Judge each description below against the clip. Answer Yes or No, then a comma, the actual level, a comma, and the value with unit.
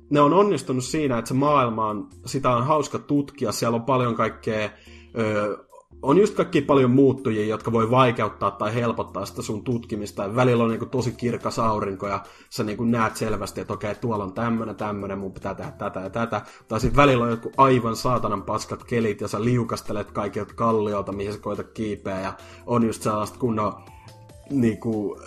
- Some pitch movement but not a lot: Yes, average, 3.3 semitones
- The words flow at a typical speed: No, fast, 190 wpm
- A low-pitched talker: Yes, low, 115 Hz